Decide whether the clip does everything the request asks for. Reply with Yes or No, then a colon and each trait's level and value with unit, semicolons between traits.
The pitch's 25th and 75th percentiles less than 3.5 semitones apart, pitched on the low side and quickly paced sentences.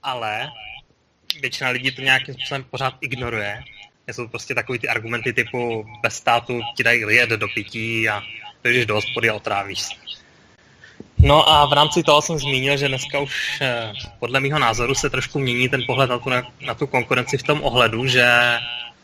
Yes: average, 2.7 semitones; low, 125 Hz; fast, 175 wpm